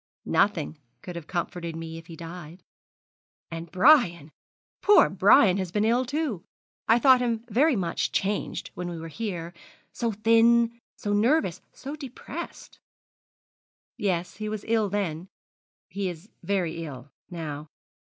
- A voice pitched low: No, high, 190 Hz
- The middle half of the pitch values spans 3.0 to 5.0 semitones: No, wide, 5.4 semitones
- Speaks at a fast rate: No, average, 140 wpm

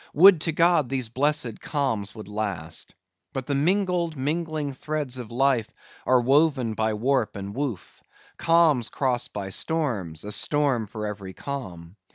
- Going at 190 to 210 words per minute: No, average, 150 wpm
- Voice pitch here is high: No, low, 130 Hz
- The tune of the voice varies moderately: No, wide, 5.7 semitones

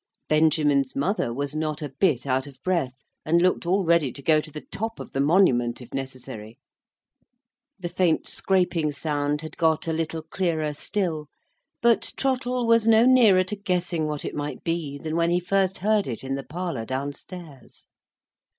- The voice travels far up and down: No, average, 4.5 semitones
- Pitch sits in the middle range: Yes, medium, 160 Hz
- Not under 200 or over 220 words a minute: No, average, 175 wpm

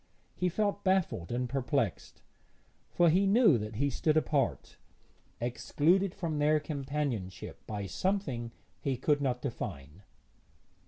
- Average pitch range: No, wide, 6.5 semitones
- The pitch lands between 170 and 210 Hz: No, medium, 140 Hz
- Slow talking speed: Yes, slow, 120 wpm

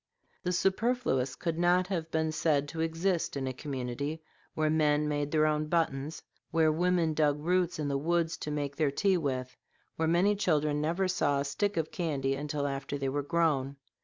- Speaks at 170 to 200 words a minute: Yes, average, 190 wpm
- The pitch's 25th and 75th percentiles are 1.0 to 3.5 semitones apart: Yes, average, 2.9 semitones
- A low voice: No, medium, 155 Hz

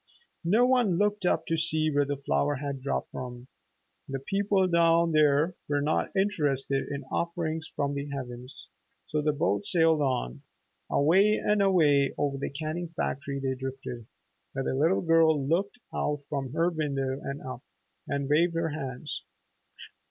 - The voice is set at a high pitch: No, medium, 150 Hz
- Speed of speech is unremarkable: Yes, average, 160 wpm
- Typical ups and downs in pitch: Yes, average, 3.5 semitones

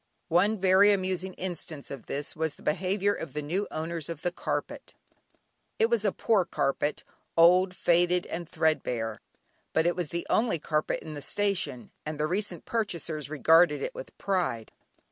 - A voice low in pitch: No, medium, 175 Hz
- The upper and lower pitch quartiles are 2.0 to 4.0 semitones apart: Yes, average, 3.7 semitones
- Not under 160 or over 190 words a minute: Yes, average, 170 wpm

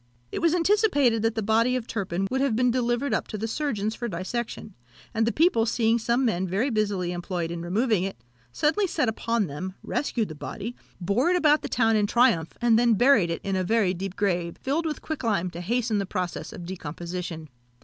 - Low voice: No, high, 220 Hz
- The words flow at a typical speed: No, fast, 210 wpm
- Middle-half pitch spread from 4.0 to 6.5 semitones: Yes, average, 4.9 semitones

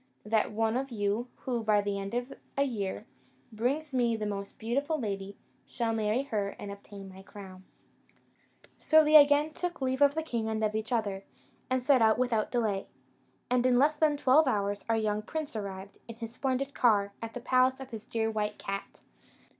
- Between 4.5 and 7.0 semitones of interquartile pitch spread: No, average, 4.1 semitones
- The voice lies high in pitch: Yes, high, 225 Hz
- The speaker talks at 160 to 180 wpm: No, average, 195 wpm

